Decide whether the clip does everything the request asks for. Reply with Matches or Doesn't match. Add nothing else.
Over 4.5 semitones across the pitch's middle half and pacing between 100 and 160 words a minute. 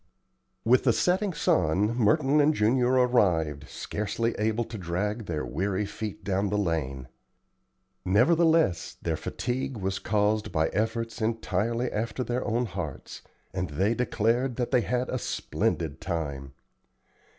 Matches